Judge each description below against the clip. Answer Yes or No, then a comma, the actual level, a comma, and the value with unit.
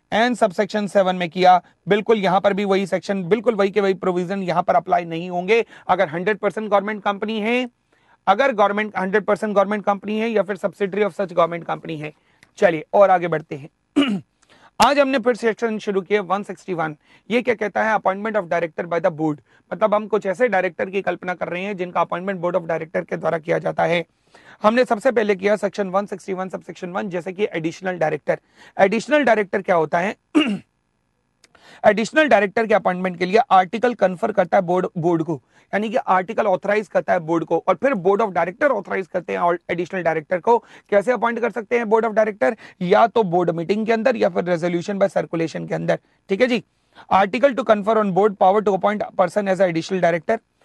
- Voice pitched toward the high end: Yes, high, 200 Hz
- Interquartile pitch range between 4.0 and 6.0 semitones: No, average, 3.2 semitones